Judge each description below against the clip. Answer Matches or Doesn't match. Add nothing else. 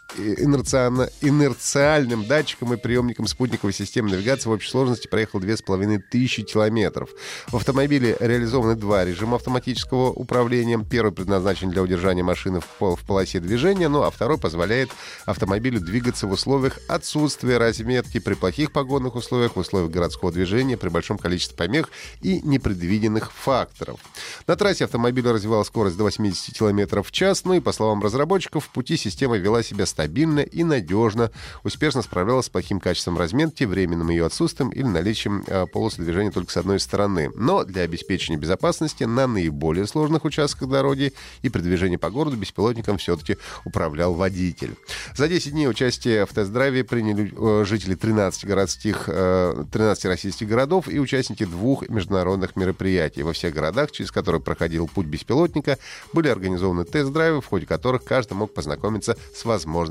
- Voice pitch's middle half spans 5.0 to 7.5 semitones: Matches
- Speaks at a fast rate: Doesn't match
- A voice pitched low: Matches